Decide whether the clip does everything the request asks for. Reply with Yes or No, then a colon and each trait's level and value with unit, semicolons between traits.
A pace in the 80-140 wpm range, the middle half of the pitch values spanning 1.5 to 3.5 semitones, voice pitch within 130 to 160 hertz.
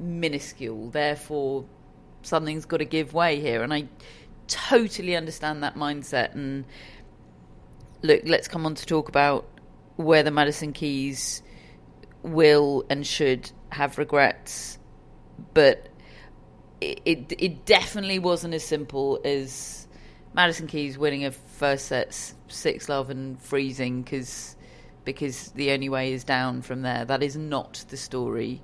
Yes: slow, 135 wpm; average, 3.0 semitones; medium, 140 Hz